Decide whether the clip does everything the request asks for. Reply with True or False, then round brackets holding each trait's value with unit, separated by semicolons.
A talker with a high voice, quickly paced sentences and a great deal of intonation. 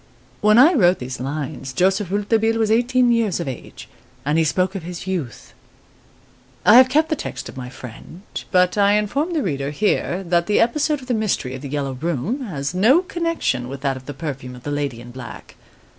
False (180 Hz; 210 wpm; 8.5 semitones)